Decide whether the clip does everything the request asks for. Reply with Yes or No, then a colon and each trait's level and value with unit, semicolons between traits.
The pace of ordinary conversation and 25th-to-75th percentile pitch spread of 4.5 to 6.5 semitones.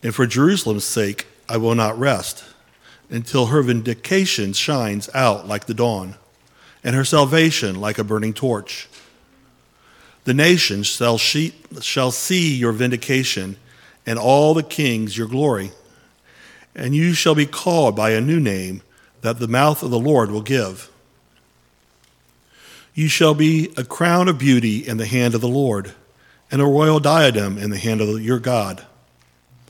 Yes: average, 150 wpm; average, 5.3 semitones